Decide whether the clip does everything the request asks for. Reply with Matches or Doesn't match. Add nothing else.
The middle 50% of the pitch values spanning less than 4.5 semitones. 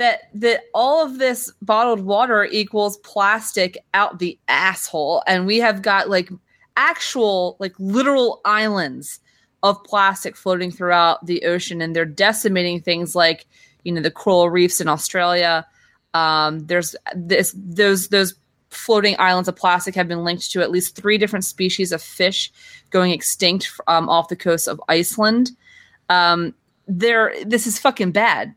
Matches